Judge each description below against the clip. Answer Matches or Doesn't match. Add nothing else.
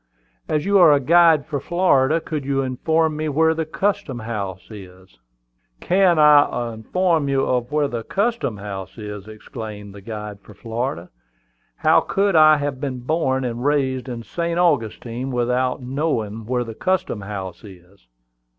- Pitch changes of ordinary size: Doesn't match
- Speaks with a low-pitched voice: Matches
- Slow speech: Doesn't match